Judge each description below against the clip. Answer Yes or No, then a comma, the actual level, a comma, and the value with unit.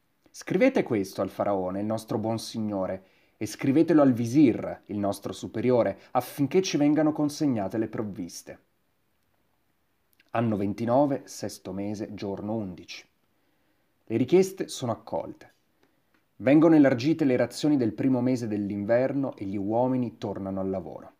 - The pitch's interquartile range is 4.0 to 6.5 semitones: Yes, average, 4.6 semitones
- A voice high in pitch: No, low, 115 Hz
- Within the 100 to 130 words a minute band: Yes, average, 125 wpm